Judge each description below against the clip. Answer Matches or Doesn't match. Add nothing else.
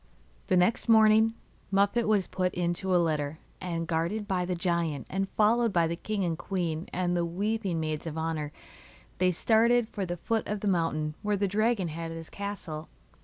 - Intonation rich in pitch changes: Doesn't match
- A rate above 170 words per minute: Matches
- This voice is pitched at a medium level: Matches